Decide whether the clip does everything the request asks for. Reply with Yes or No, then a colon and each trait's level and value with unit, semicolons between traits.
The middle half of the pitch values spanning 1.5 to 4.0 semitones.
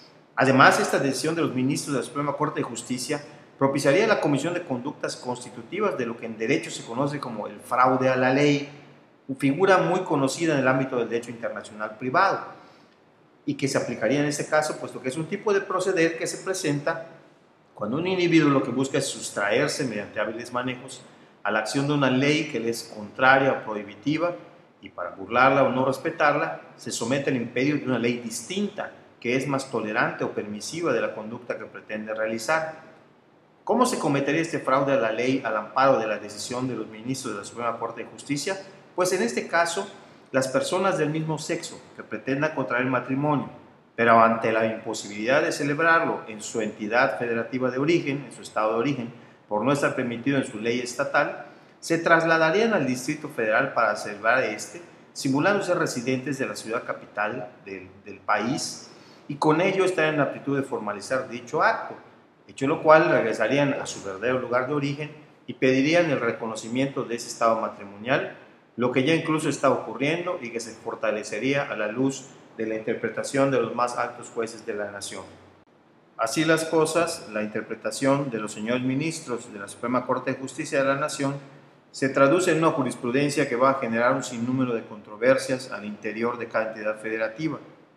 No: average, 4.7 semitones